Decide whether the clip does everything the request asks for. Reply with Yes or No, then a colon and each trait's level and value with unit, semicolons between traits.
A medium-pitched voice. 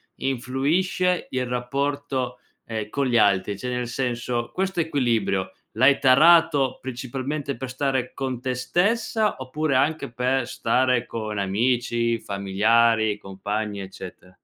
No: low, 125 Hz